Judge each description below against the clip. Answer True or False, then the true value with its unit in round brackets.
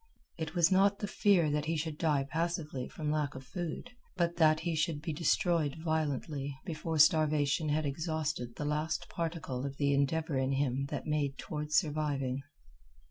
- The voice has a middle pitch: True (155 Hz)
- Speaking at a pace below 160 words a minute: False (170 wpm)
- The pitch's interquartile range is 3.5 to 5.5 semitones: False (2.5 semitones)